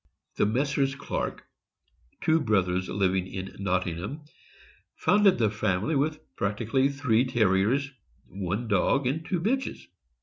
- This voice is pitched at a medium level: No, low, 115 Hz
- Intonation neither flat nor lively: No, wide, 6.6 semitones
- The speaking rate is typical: No, slow, 125 wpm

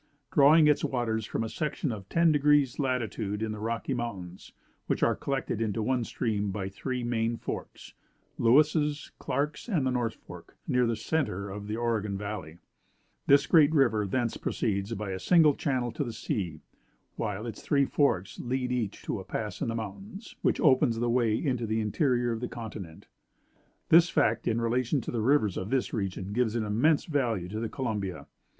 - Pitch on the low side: Yes, low, 115 Hz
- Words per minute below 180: No, average, 185 wpm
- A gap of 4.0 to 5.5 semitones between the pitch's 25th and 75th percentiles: Yes, average, 4.3 semitones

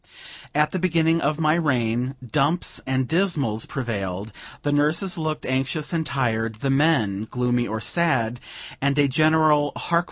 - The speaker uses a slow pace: No, average, 150 wpm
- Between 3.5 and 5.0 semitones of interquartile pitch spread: Yes, average, 4.7 semitones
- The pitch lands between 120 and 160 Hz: Yes, medium, 140 Hz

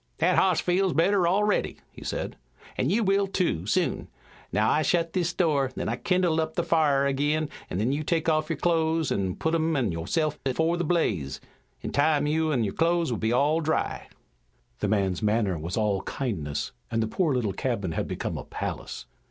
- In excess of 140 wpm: Yes, average, 195 wpm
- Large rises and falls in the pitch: Yes, wide, 7.1 semitones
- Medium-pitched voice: Yes, medium, 150 Hz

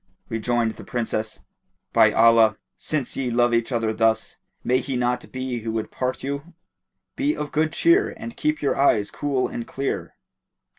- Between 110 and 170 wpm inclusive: Yes, average, 165 wpm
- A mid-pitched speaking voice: No, low, 125 Hz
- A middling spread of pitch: Yes, average, 3.7 semitones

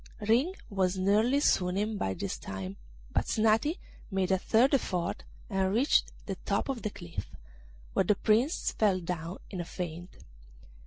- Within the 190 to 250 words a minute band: No, average, 155 wpm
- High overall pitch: Yes, high, 195 Hz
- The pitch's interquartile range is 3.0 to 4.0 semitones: Yes, average, 3.7 semitones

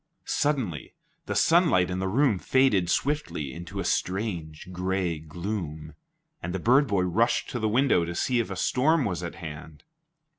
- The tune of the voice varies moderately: No, wide, 6.1 semitones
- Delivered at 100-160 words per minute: No, average, 170 wpm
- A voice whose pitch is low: Yes, very low, 95 Hz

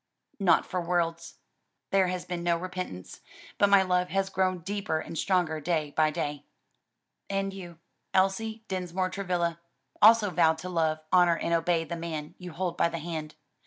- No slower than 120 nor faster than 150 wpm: No, average, 165 wpm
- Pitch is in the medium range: Yes, medium, 175 Hz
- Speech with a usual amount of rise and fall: No, narrow, 2.3 semitones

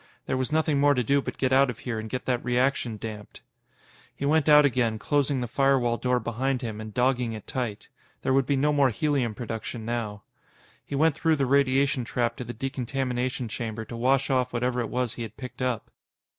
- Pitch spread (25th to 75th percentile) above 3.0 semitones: No, average, 2.7 semitones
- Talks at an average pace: No, fast, 210 wpm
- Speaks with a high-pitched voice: No, low, 125 Hz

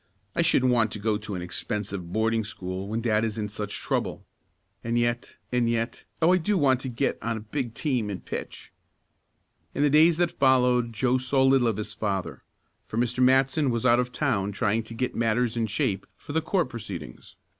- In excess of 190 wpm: Yes, fast, 205 wpm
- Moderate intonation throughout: Yes, average, 3.3 semitones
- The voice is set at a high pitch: No, low, 115 Hz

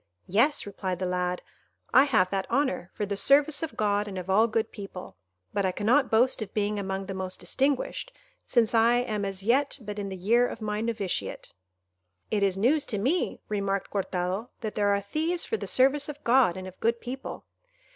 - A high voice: Yes, high, 210 Hz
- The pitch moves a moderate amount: Yes, average, 4.3 semitones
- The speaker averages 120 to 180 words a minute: No, average, 200 wpm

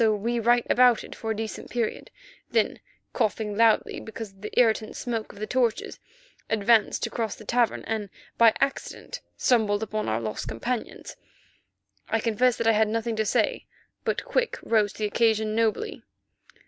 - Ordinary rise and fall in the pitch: No, narrow, 1.8 semitones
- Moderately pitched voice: No, high, 225 Hz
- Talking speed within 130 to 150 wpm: No, average, 160 wpm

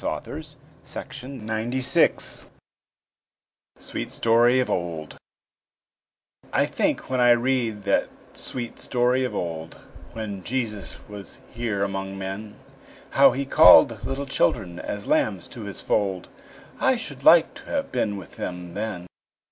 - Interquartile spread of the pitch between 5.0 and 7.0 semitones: No, average, 4.5 semitones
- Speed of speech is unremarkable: No, slow, 125 wpm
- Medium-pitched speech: No, low, 110 Hz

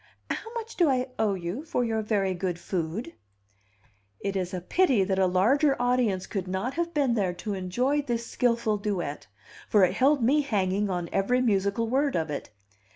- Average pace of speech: Yes, average, 185 wpm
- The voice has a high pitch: Yes, high, 210 Hz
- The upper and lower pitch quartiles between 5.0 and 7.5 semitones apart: Yes, average, 5.3 semitones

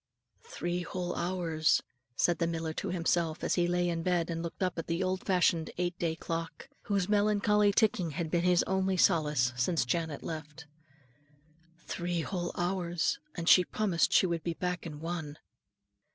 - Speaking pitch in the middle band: Yes, medium, 175 Hz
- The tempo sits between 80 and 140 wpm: No, average, 170 wpm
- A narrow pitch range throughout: Yes, narrow, 1.8 semitones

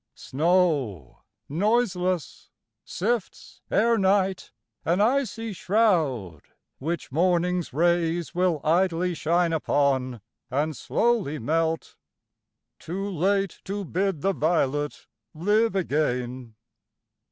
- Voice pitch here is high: No, medium, 175 Hz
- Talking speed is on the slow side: Yes, slow, 85 wpm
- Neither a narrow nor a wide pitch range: Yes, average, 4.6 semitones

